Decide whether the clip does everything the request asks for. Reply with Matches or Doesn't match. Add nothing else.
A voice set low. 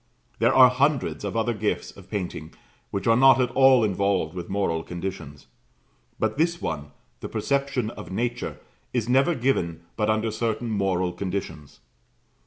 Matches